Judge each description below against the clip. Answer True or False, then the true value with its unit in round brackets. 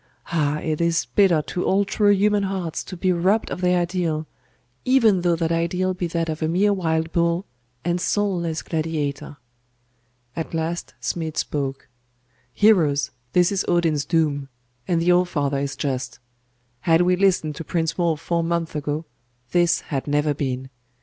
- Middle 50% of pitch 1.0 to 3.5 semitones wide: True (2.8 semitones)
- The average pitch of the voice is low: False (170 Hz)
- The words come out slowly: False (165 wpm)